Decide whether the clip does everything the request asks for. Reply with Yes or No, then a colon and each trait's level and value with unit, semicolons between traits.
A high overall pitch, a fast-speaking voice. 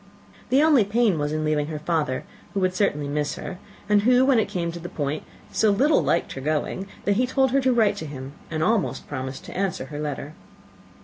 No: medium, 180 Hz; fast, 225 wpm